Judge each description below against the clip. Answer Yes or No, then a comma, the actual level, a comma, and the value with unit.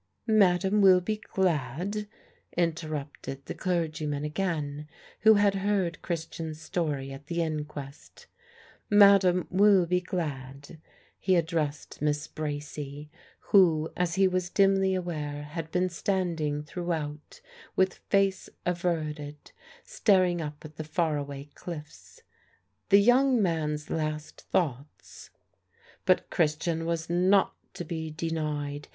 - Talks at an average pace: No, slow, 120 wpm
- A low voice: No, medium, 165 Hz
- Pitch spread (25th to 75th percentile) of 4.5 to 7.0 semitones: No, average, 3.7 semitones